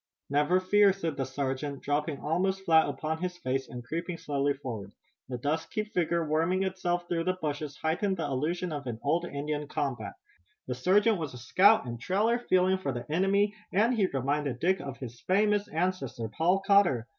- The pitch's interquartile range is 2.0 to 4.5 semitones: No, average, 5.1 semitones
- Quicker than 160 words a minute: Yes, average, 180 wpm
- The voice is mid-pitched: Yes, medium, 160 Hz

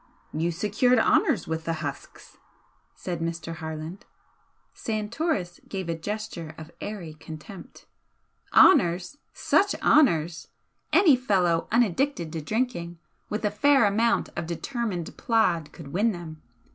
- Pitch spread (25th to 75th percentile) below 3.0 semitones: No, wide, 5.4 semitones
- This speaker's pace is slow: Yes, slow, 120 wpm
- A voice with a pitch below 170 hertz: No, medium, 180 Hz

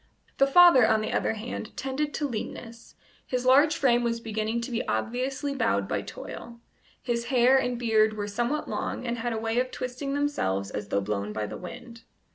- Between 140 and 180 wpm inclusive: No, average, 195 wpm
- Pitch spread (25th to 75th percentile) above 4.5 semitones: No, average, 3.2 semitones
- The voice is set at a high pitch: Yes, high, 235 Hz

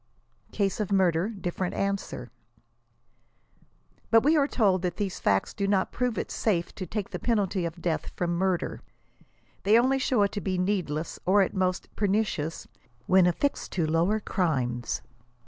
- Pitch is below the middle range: No, high, 190 Hz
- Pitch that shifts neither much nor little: Yes, average, 3.2 semitones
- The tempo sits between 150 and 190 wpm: Yes, average, 160 wpm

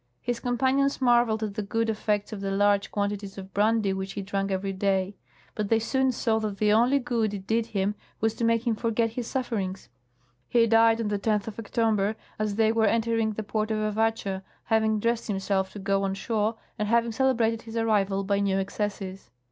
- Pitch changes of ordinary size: No, narrow, 2.3 semitones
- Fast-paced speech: Yes, fast, 210 wpm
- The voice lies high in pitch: Yes, high, 215 Hz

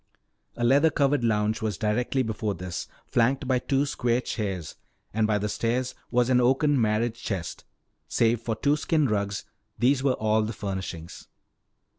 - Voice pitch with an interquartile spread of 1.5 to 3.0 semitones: No, average, 3.5 semitones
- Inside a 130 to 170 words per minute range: Yes, average, 160 wpm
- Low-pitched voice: Yes, low, 115 Hz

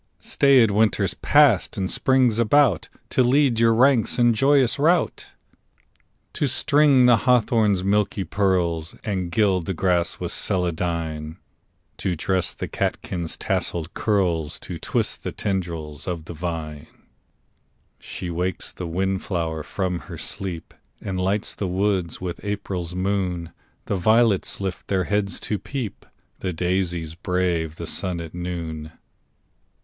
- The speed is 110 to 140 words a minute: Yes, slow, 135 wpm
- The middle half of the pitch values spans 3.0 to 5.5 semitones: Yes, average, 4.1 semitones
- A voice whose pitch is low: Yes, very low, 95 Hz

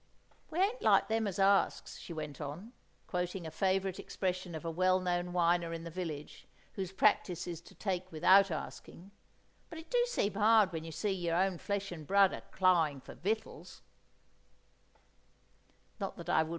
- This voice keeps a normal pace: Yes, average, 165 wpm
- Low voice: No, medium, 185 Hz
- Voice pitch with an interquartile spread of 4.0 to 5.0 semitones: No, average, 2.8 semitones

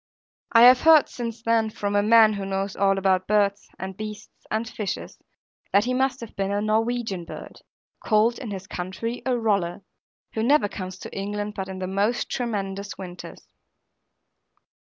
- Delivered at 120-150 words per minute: No, average, 170 wpm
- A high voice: Yes, high, 210 Hz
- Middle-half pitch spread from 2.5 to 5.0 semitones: Yes, average, 2.9 semitones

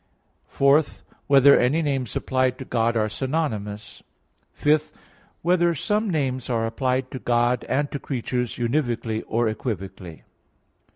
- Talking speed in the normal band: No, slow, 125 wpm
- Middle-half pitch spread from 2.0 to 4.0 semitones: Yes, average, 3.7 semitones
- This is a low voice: Yes, low, 130 Hz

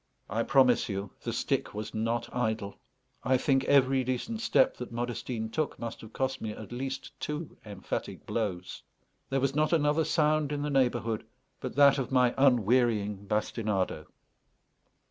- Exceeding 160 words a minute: No, average, 155 wpm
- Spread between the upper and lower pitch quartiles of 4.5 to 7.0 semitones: No, average, 3.9 semitones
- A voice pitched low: Yes, low, 125 Hz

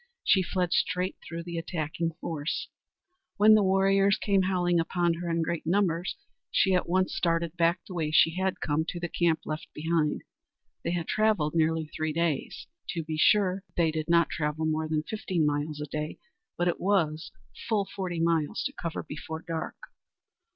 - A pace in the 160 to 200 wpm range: Yes, average, 180 wpm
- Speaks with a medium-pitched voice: Yes, medium, 170 Hz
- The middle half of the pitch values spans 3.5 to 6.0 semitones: No, average, 2.7 semitones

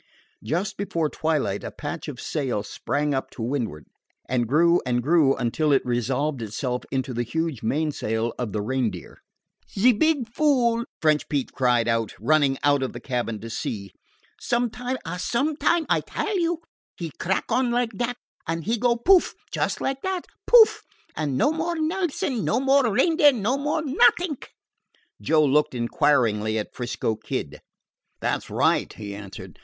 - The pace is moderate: Yes, average, 160 wpm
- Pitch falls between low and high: Yes, medium, 155 Hz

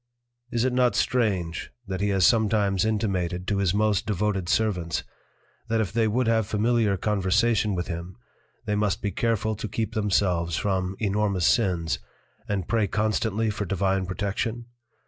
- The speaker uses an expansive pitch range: No, average, 2.8 semitones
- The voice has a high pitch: No, low, 105 Hz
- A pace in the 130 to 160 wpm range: Yes, average, 155 wpm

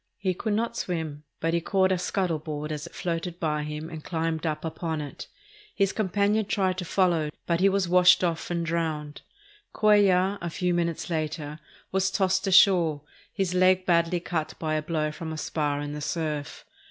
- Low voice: No, medium, 170 Hz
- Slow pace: No, average, 190 wpm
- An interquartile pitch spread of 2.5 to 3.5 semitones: Yes, average, 3.1 semitones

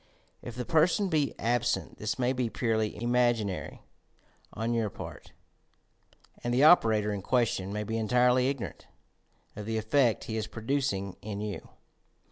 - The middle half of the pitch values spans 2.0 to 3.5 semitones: Yes, average, 2.7 semitones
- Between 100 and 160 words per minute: Yes, average, 155 wpm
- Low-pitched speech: Yes, low, 115 Hz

